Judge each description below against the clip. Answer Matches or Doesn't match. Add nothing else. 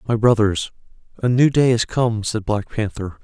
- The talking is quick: Doesn't match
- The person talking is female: Doesn't match